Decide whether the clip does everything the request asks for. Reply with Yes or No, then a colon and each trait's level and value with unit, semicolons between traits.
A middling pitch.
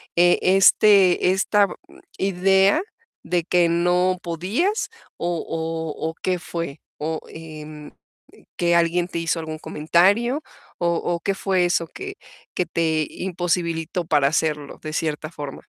Yes: medium, 170 Hz